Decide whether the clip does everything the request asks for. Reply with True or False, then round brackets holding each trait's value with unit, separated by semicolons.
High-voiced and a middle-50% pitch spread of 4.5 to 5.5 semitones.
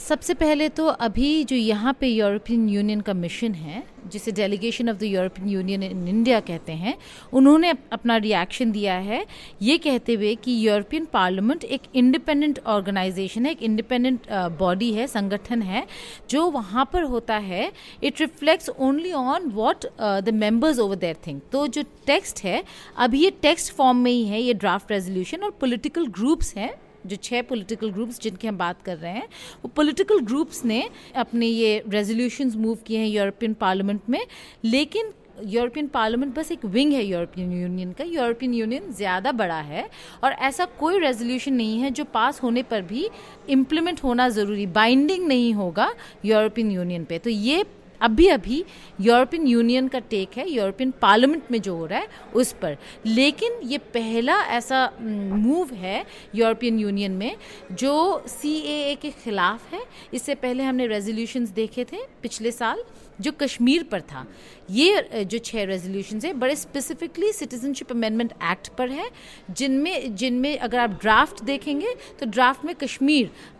True (240 Hz; 5.0 semitones)